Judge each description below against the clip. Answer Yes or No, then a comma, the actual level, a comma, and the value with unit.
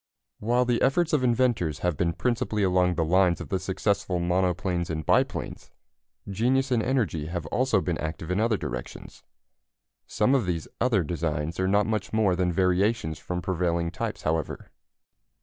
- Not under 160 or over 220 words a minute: Yes, average, 165 wpm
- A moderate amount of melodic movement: Yes, average, 4.7 semitones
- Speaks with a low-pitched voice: Yes, very low, 90 Hz